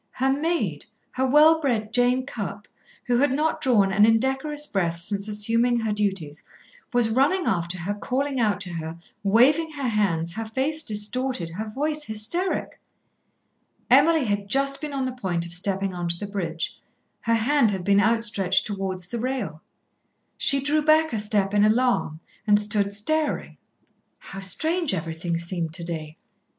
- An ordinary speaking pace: Yes, average, 160 wpm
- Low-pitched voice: No, high, 215 Hz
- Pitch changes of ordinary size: No, wide, 5.7 semitones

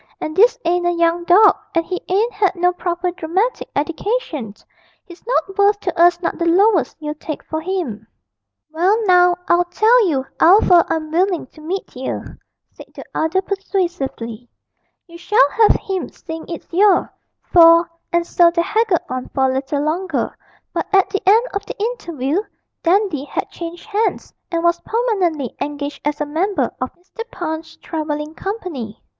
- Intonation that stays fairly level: No, average, 3.6 semitones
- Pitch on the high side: Yes, very high, 345 Hz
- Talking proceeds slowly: No, average, 170 wpm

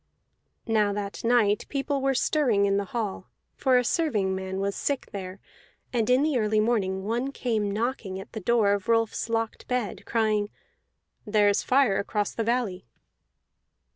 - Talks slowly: No, average, 160 wpm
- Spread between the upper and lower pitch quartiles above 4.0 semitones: No, average, 3.4 semitones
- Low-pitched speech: No, high, 220 Hz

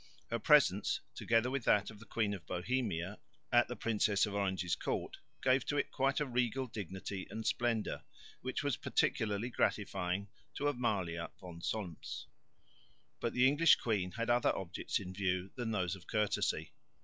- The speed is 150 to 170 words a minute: Yes, average, 160 wpm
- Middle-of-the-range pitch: No, low, 105 Hz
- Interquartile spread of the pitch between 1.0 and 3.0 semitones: No, average, 4.5 semitones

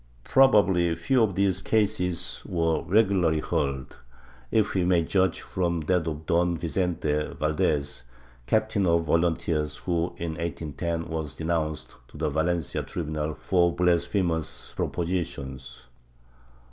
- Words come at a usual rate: No, slow, 120 wpm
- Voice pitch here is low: Yes, very low, 85 Hz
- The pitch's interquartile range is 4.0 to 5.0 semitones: No, narrow, 2.6 semitones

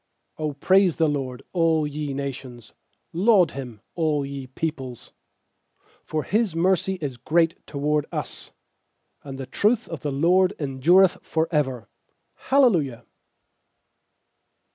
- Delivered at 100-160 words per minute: Yes, average, 140 wpm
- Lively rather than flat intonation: No, average, 4.3 semitones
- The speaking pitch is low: No, medium, 150 Hz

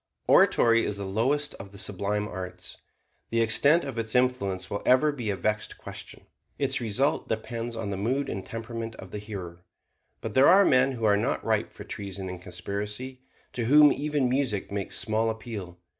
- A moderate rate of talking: Yes, average, 185 wpm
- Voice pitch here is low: Yes, low, 110 Hz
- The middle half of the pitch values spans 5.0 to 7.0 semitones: No, average, 4.2 semitones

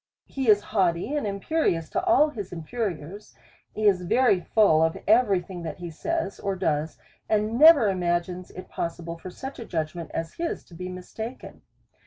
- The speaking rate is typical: Yes, average, 180 wpm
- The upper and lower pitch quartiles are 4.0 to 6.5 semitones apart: Yes, average, 4.8 semitones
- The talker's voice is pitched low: No, high, 190 Hz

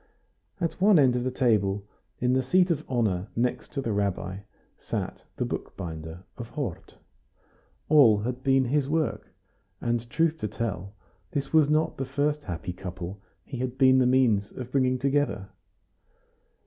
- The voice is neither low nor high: No, low, 125 Hz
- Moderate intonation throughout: No, wide, 5.7 semitones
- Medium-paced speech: Yes, average, 160 wpm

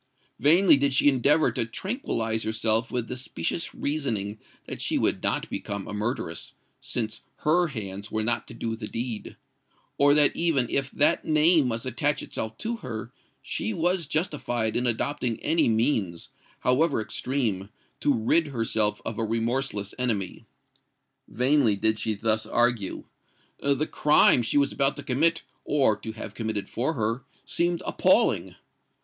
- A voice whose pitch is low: Yes, low, 120 Hz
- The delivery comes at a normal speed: Yes, average, 145 wpm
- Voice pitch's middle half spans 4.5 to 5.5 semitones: Yes, average, 4.9 semitones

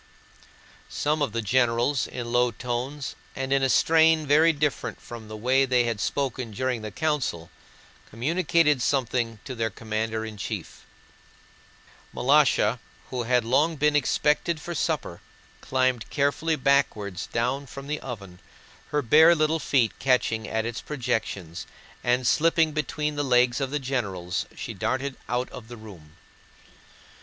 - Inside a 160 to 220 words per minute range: No, average, 145 wpm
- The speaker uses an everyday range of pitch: Yes, average, 4.4 semitones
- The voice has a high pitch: No, low, 130 Hz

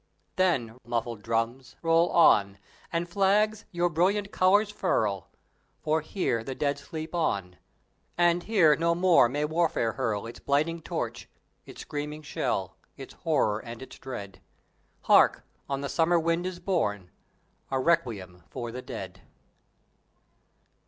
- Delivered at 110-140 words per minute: Yes, slow, 135 wpm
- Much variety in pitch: Yes, wide, 7.0 semitones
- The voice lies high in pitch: No, medium, 150 Hz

